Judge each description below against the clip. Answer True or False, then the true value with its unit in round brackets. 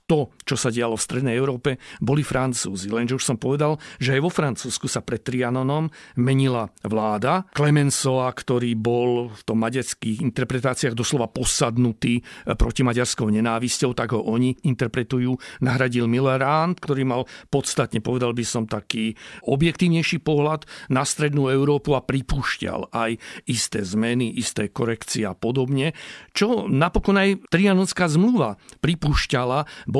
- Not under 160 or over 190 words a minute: False (135 wpm)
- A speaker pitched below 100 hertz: False (130 Hz)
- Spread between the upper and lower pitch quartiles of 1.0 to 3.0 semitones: False (3.5 semitones)